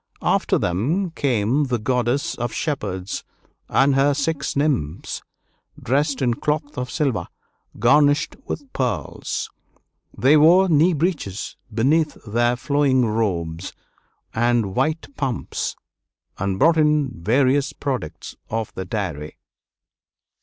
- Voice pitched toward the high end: No, low, 130 Hz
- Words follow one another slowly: Yes, slow, 110 wpm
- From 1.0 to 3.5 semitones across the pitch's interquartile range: No, average, 5.2 semitones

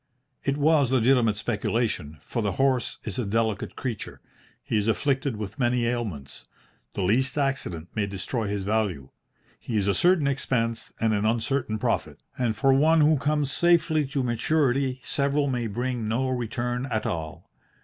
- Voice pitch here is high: No, low, 120 Hz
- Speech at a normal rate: Yes, average, 160 wpm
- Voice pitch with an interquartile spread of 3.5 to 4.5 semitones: Yes, average, 4.2 semitones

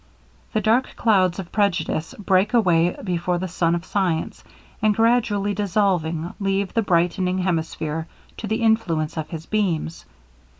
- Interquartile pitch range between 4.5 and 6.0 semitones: No, average, 3.8 semitones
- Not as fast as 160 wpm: Yes, average, 140 wpm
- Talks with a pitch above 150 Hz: Yes, medium, 185 Hz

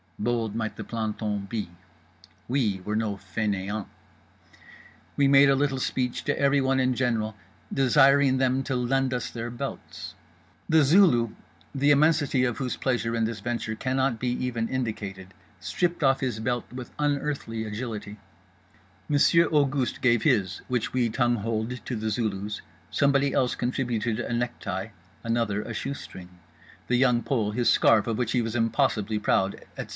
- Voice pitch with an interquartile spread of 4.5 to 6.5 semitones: No, average, 3.7 semitones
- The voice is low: Yes, low, 120 Hz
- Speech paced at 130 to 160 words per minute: Yes, average, 145 wpm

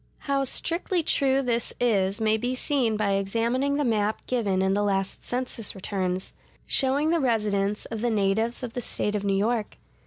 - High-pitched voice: Yes, high, 225 Hz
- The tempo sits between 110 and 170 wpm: No, average, 180 wpm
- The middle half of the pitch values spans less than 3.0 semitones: No, average, 4.1 semitones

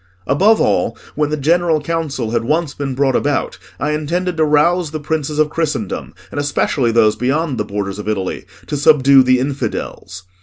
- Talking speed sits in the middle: Yes, average, 180 wpm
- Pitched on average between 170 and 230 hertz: No, medium, 145 Hz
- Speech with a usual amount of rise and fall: Yes, average, 3.9 semitones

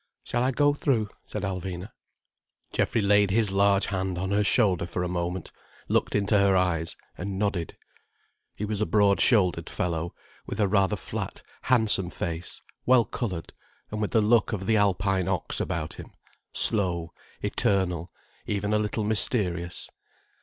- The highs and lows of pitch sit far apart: No, average, 3.0 semitones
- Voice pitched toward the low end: Yes, low, 100 Hz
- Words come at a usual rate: Yes, average, 155 wpm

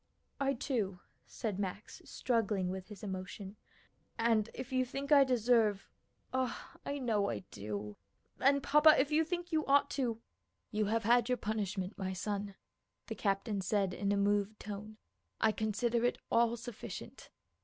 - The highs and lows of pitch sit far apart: No, average, 4.0 semitones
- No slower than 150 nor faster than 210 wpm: Yes, average, 160 wpm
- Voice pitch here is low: No, high, 220 Hz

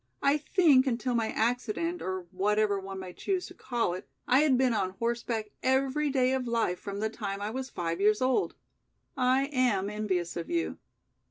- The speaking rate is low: No, average, 185 wpm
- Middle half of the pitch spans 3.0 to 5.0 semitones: Yes, average, 4.7 semitones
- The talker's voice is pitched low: No, high, 235 Hz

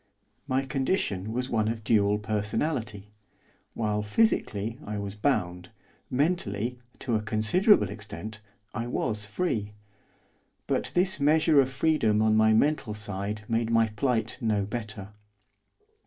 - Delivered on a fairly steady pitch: No, average, 3.7 semitones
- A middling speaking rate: No, slow, 125 wpm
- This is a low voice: Yes, low, 110 Hz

